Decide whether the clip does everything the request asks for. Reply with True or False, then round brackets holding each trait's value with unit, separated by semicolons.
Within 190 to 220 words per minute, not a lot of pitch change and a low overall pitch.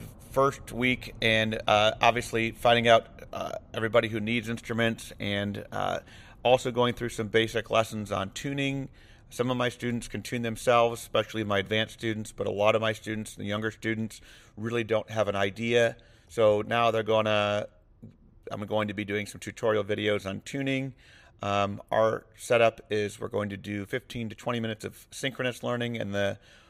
False (175 wpm; 2.1 semitones; 110 Hz)